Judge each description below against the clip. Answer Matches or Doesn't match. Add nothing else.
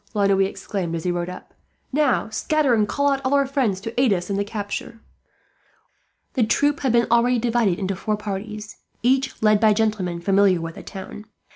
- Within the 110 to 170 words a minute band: Doesn't match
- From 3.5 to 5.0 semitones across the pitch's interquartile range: Matches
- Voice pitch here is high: Matches